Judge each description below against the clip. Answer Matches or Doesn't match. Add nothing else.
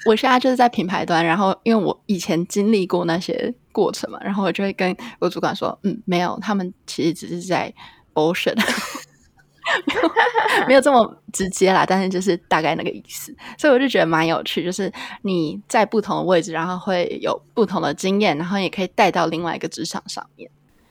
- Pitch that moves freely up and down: Doesn't match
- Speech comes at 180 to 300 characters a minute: Doesn't match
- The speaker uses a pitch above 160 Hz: Matches